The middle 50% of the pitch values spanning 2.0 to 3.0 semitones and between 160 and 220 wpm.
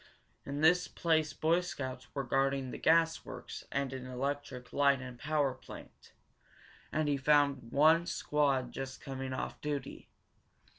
No: narrow, 2.6 semitones; average, 145 wpm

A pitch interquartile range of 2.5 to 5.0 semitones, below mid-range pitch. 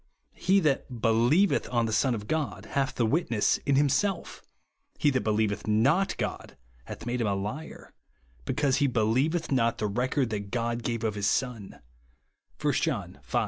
Yes: average, 4.4 semitones; low, 120 Hz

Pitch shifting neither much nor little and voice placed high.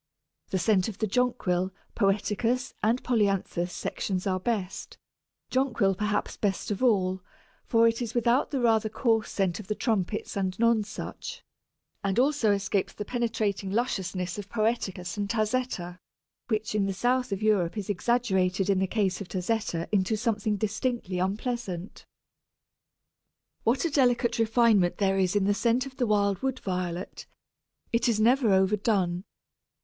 Yes: average, 3.5 semitones; high, 210 Hz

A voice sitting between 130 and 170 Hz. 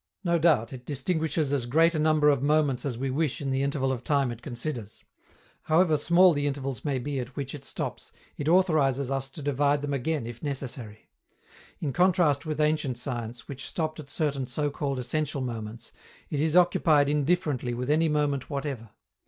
Yes: medium, 140 Hz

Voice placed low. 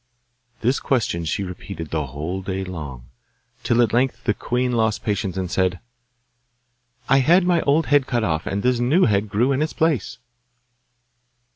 Yes: low, 110 Hz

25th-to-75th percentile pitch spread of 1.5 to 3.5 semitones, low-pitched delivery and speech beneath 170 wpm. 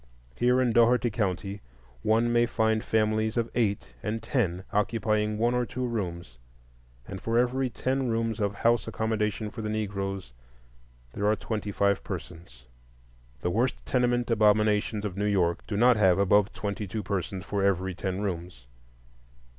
Yes: average, 2.8 semitones; low, 105 Hz; average, 155 wpm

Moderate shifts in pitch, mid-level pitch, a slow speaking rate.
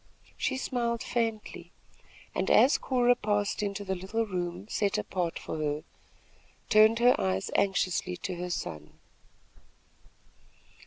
No: average, 4.3 semitones; high, 200 Hz; slow, 120 wpm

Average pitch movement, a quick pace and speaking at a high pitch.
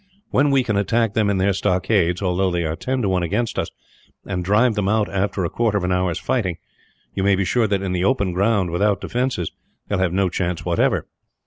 No: average, 3.2 semitones; fast, 230 wpm; low, 100 Hz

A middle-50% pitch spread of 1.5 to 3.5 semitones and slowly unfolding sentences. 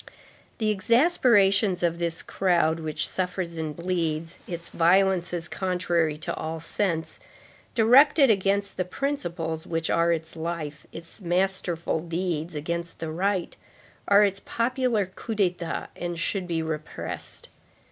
Yes: average, 3.2 semitones; slow, 125 wpm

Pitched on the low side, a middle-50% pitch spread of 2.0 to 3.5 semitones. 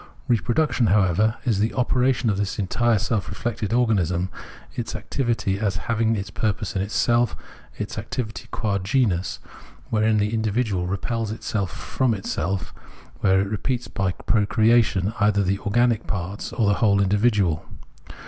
Yes: low, 105 Hz; average, 2.8 semitones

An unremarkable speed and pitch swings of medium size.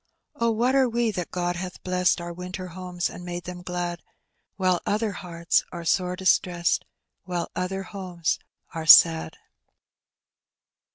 No: average, 145 wpm; narrow, 1.4 semitones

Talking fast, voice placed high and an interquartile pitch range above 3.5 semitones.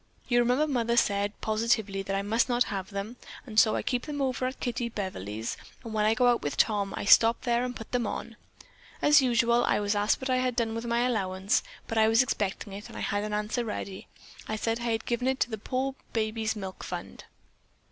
No: fast, 230 wpm; high, 225 Hz; average, 3.0 semitones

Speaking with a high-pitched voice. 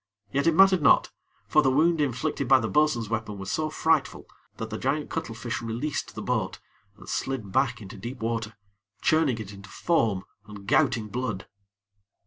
No: low, 120 Hz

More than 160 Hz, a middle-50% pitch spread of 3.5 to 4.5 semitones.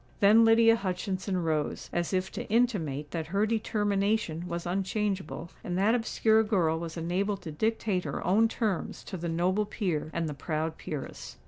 Yes: medium, 185 Hz; average, 4.2 semitones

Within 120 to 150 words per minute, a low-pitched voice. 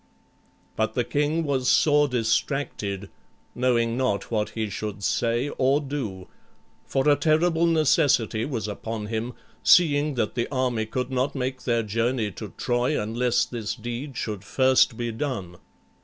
Yes: average, 145 wpm; low, 125 Hz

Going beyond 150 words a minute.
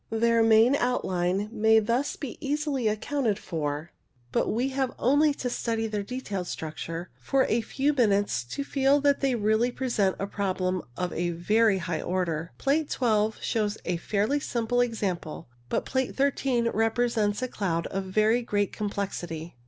Yes: average, 160 wpm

